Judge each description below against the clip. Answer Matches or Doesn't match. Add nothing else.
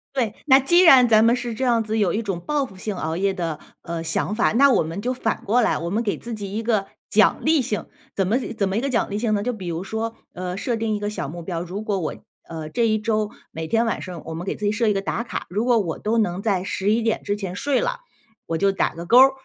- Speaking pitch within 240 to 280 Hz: Doesn't match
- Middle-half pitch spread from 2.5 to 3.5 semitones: Doesn't match